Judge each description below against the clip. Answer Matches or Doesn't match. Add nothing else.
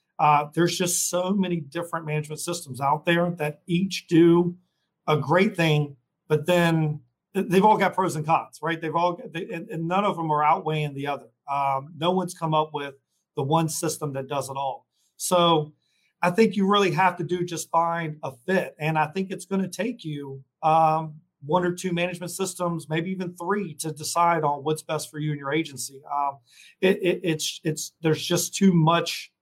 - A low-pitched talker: Doesn't match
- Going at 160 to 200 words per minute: Matches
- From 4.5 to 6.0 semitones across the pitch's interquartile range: Doesn't match